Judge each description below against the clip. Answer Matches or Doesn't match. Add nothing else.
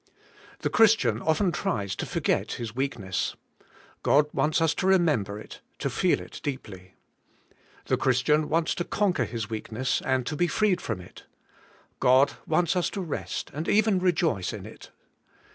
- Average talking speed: Matches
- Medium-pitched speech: Matches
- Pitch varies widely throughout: Matches